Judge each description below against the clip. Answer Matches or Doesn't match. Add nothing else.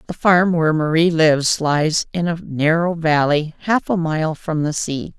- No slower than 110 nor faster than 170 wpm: Doesn't match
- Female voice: Matches